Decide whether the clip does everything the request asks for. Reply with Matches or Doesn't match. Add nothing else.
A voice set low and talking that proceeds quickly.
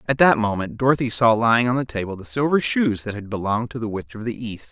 Matches